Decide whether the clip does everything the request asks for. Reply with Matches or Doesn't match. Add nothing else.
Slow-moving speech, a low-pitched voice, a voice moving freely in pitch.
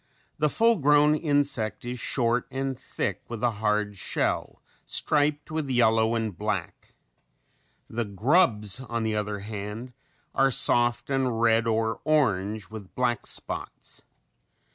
Doesn't match